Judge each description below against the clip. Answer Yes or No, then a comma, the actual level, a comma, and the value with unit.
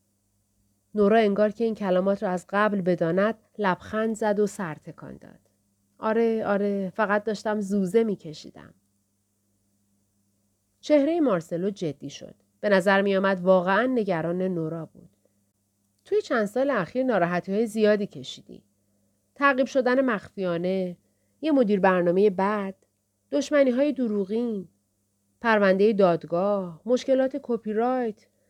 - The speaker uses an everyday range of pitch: No, wide, 6.1 semitones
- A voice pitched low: No, high, 195 Hz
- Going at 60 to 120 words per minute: Yes, average, 110 wpm